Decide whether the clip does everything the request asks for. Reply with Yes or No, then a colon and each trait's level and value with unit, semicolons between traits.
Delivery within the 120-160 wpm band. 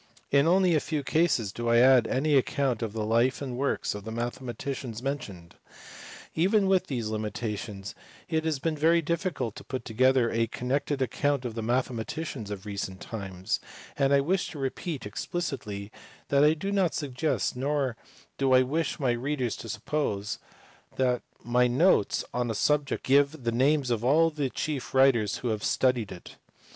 No: average, 175 wpm